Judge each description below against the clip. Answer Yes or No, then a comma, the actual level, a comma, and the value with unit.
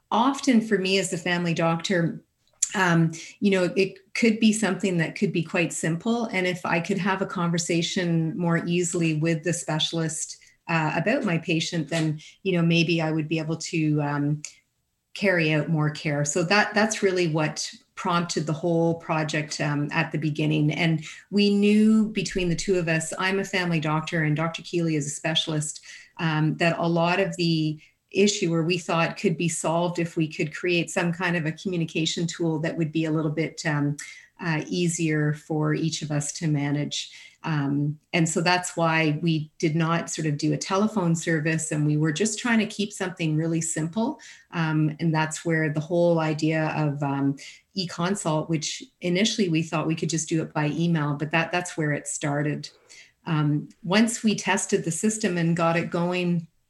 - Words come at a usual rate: Yes, average, 190 wpm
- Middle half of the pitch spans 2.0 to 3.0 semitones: Yes, narrow, 2.6 semitones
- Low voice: No, medium, 165 Hz